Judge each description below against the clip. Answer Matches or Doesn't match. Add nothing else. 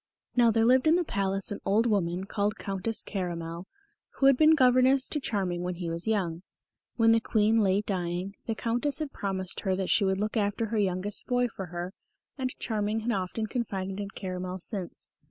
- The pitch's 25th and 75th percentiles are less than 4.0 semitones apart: Matches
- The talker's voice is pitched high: Matches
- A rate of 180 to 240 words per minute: Matches